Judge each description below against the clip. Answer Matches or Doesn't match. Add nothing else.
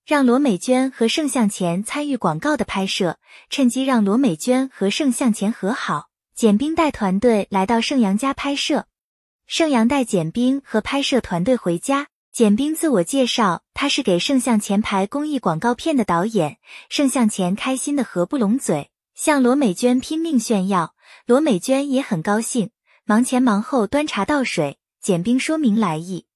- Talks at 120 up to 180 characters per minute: Doesn't match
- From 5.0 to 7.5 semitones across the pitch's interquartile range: Matches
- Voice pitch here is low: Doesn't match